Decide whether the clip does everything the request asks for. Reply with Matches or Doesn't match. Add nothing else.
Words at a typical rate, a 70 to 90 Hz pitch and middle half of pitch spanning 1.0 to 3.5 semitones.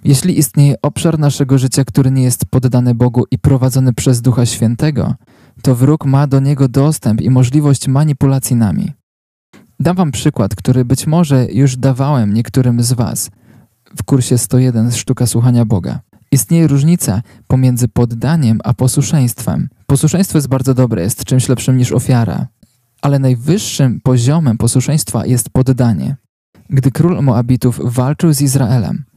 Doesn't match